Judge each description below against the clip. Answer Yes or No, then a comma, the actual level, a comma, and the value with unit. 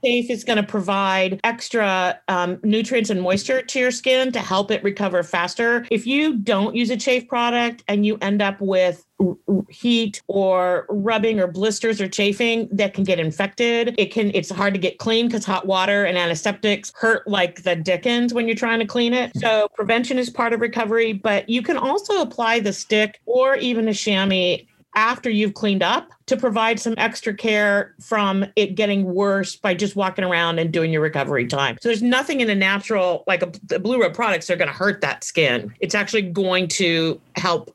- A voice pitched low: No, high, 210 Hz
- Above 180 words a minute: Yes, average, 200 wpm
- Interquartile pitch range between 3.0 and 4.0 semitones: Yes, average, 3.4 semitones